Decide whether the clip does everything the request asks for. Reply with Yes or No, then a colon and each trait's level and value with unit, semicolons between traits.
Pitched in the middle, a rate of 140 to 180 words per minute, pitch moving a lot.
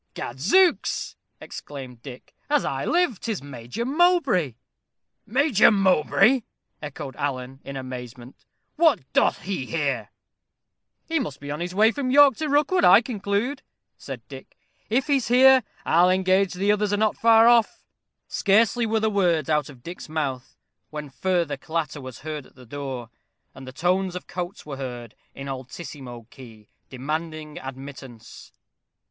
Yes: medium, 170 Hz; average, 150 wpm; wide, 8.8 semitones